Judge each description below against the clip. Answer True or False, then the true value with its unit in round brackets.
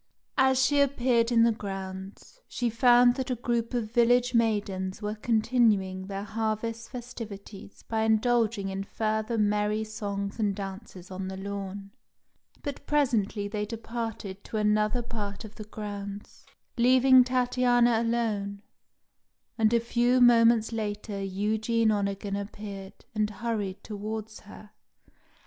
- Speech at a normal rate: False (130 wpm)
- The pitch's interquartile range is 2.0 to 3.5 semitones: True (2.7 semitones)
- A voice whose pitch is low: False (215 Hz)